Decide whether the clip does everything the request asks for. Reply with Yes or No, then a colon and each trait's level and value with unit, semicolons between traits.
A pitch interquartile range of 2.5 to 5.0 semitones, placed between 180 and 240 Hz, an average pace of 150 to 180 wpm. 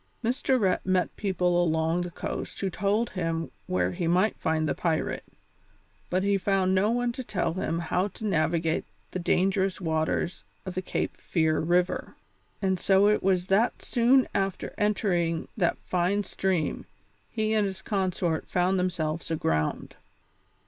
Yes: average, 2.8 semitones; medium, 185 Hz; average, 155 wpm